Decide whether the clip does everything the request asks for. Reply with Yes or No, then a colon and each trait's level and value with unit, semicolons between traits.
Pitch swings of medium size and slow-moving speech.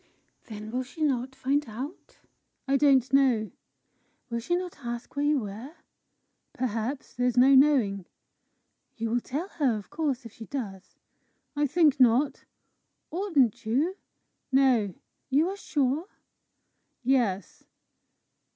Yes: average, 3.9 semitones; slow, 130 wpm